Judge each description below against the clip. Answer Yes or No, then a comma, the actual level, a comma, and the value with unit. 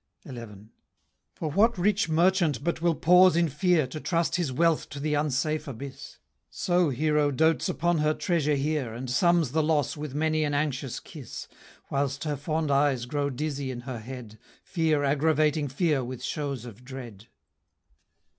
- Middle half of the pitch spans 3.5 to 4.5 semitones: No, average, 3.1 semitones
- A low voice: No, medium, 150 Hz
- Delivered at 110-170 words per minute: Yes, average, 165 wpm